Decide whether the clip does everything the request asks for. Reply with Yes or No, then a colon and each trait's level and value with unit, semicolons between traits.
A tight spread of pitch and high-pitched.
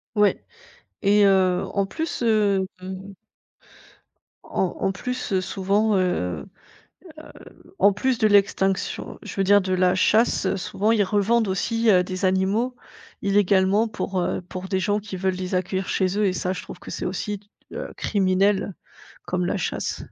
Yes: narrow, 1.9 semitones; high, 195 Hz